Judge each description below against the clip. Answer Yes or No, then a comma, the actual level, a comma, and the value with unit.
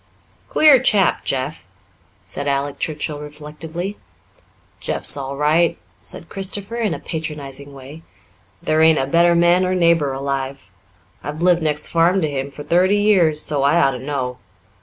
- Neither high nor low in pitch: Yes, medium, 155 Hz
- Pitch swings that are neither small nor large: Yes, average, 3.7 semitones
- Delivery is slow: No, average, 155 wpm